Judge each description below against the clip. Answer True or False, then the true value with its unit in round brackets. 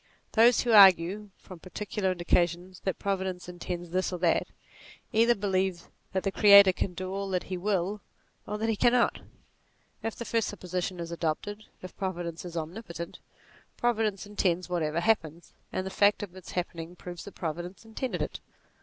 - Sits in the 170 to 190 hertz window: True (185 Hz)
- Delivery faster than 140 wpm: True (165 wpm)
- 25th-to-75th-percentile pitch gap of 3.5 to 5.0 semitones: False (3.0 semitones)